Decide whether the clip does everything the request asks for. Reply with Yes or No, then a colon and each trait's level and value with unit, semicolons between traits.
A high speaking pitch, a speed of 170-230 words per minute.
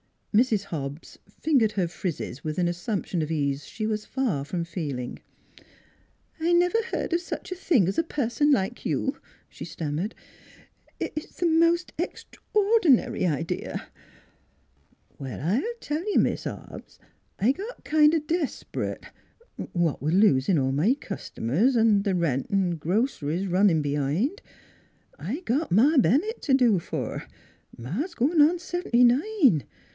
No: high, 215 Hz; average, 155 wpm